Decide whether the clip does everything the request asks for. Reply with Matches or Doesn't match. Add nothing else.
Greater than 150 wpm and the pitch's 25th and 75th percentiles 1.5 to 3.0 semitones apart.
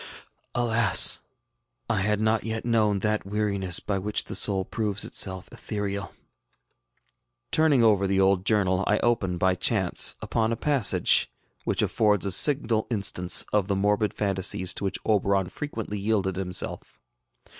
Doesn't match